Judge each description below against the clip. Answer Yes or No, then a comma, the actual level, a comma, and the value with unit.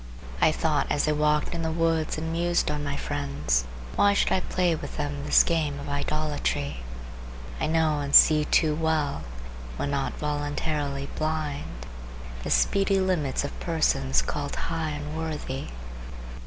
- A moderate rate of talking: Yes, average, 155 wpm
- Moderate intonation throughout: No, narrow, 2.1 semitones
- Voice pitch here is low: No, medium, 150 Hz